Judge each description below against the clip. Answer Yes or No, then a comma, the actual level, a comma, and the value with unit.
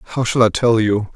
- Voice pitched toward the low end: Yes, low, 115 Hz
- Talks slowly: No, fast, 260 wpm